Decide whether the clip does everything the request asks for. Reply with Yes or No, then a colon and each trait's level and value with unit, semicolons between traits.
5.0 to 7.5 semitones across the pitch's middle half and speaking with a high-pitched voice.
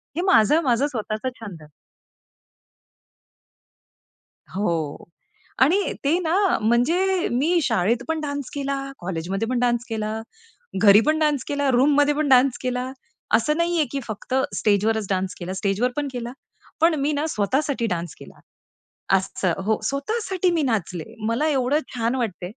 Yes: wide, 5.4 semitones; very high, 250 Hz